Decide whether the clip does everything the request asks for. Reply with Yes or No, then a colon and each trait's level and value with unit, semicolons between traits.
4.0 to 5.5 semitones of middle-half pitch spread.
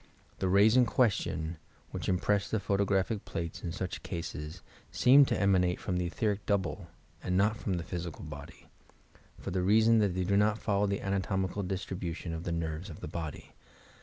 No: average, 3.0 semitones